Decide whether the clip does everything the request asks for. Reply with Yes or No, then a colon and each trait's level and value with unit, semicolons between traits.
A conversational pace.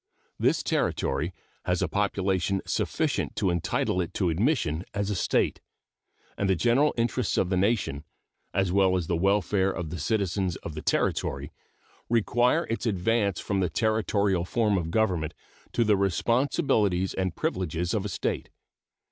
Yes: average, 155 wpm